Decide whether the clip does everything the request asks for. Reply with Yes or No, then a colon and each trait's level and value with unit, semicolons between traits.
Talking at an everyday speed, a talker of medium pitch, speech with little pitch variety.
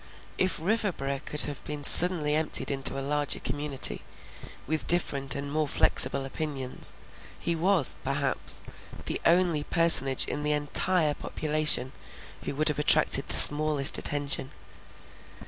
No: slow, 130 wpm; medium, 150 Hz; narrow, 2.2 semitones